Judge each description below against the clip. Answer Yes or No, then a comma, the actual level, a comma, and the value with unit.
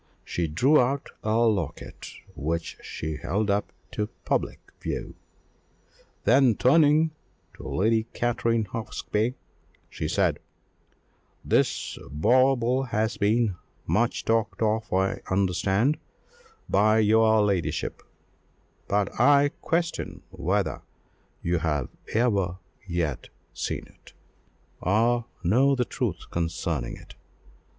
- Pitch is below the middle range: Yes, low, 110 Hz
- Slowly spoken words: Yes, slow, 105 wpm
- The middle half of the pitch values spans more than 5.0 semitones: No, average, 4.5 semitones